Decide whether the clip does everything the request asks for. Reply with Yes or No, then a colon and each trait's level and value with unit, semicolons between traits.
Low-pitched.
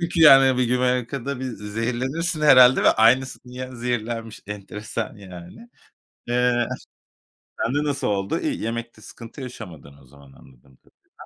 Yes: low, 120 Hz